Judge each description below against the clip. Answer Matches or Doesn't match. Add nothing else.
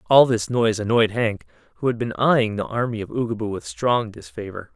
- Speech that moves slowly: Doesn't match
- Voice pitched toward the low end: Matches